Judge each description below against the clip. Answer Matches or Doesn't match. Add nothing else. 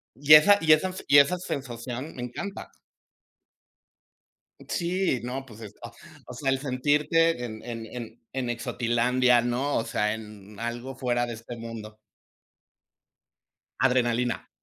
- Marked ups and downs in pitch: Doesn't match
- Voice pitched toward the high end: Doesn't match